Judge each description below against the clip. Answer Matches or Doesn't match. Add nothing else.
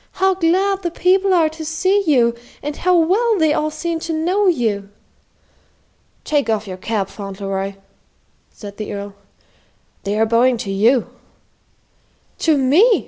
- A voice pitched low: Doesn't match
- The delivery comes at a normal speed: Matches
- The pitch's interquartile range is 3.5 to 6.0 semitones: Doesn't match